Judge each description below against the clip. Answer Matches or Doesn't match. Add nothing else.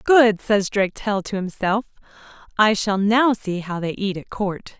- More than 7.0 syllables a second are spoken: Doesn't match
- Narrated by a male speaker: Doesn't match